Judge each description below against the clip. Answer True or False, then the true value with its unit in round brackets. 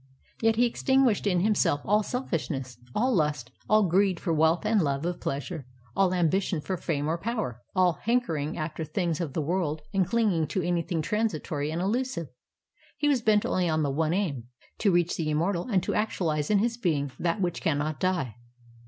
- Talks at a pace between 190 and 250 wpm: True (195 wpm)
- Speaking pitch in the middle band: True (175 Hz)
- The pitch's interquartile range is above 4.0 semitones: True (5.2 semitones)